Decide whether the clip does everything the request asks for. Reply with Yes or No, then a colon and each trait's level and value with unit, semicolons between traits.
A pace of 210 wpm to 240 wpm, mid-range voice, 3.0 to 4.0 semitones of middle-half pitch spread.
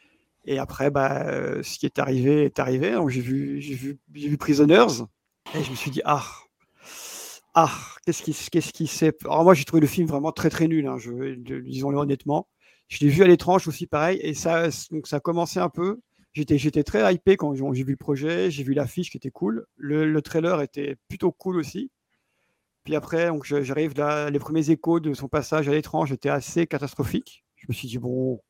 No: average, 215 wpm; medium, 150 Hz; narrow, 2.6 semitones